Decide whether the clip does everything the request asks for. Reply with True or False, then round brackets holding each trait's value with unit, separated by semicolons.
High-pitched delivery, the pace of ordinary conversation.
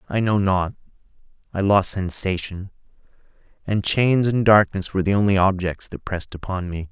False (95 Hz; 155 wpm)